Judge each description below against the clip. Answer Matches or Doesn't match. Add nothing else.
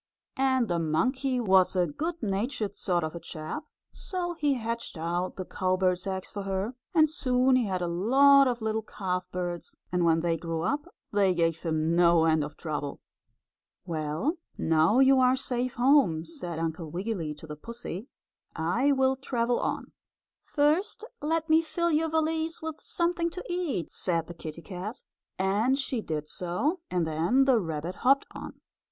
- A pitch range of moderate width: Doesn't match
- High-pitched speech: Matches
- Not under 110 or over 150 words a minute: Doesn't match